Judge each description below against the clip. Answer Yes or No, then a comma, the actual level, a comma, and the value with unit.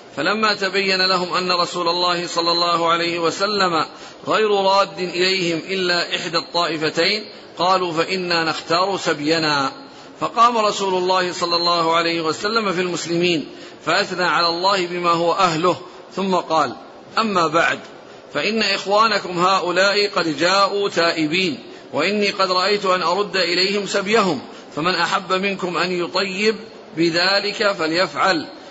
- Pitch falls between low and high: Yes, medium, 180 Hz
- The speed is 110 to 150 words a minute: Yes, average, 125 wpm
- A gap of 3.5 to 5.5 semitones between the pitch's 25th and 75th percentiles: No, narrow, 2.5 semitones